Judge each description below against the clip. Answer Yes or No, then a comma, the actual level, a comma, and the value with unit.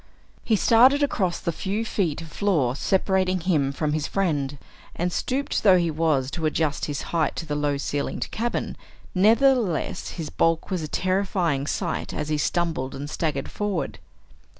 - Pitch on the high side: No, medium, 170 Hz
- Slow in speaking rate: No, average, 165 wpm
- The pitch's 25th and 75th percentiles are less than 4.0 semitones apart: No, average, 4.7 semitones